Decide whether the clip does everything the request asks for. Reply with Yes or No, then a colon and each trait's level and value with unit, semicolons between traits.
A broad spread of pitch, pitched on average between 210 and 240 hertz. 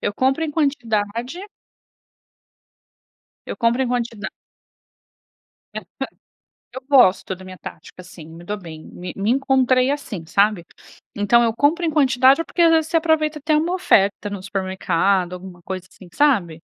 Yes: wide, 7.4 semitones; high, 230 Hz